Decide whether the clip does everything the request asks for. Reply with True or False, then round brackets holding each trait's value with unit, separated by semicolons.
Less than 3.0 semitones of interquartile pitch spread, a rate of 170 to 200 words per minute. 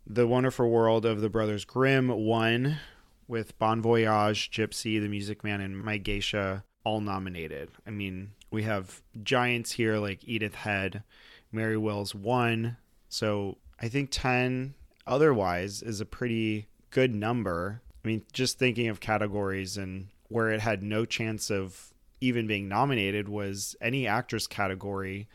False (2.5 semitones; 145 wpm)